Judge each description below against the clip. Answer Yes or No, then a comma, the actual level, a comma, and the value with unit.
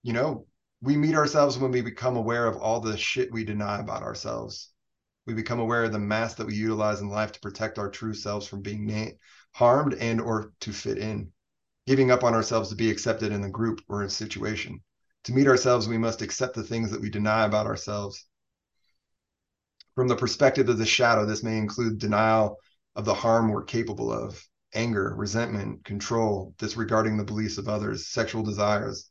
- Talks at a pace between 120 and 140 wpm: No, average, 195 wpm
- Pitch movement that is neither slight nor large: No, narrow, 1.9 semitones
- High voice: No, low, 110 Hz